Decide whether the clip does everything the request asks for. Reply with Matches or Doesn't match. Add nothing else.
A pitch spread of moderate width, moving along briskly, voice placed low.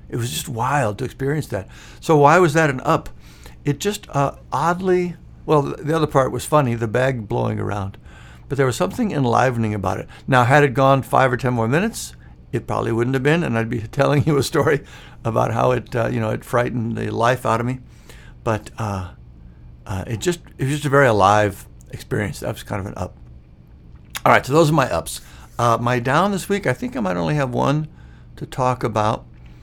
Doesn't match